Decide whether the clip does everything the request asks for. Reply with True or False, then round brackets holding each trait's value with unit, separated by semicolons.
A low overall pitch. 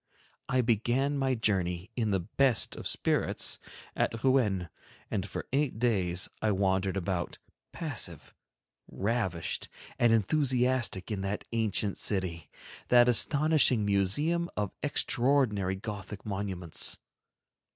True (105 Hz)